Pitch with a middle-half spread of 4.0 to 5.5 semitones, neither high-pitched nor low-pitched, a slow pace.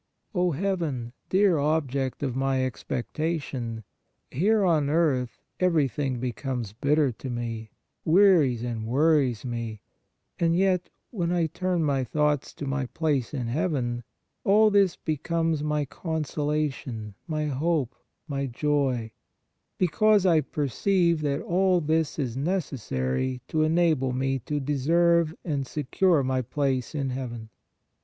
Yes: average, 4.5 semitones; medium, 145 Hz; slow, 130 wpm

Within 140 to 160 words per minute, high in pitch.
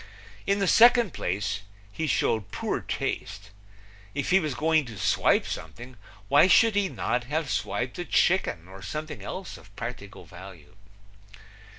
No: average, 150 wpm; low, 125 Hz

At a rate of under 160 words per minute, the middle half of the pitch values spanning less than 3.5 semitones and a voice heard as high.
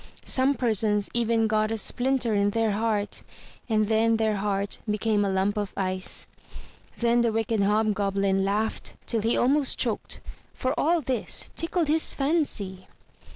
Yes: average, 150 wpm; average, 2.8 semitones; high, 220 Hz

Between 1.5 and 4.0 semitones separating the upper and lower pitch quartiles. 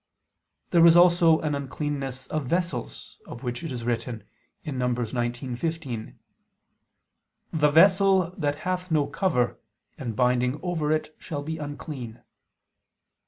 No: average, 4.9 semitones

